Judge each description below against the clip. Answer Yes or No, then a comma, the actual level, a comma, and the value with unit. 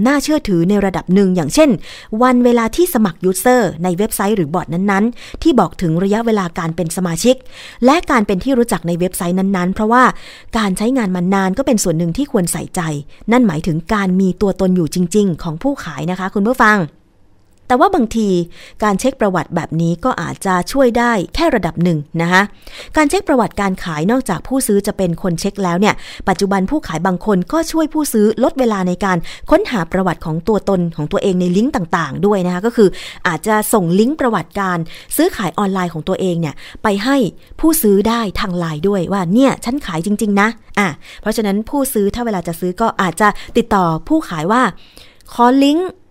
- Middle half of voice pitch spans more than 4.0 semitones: Yes, average, 4.7 semitones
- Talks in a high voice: Yes, high, 200 Hz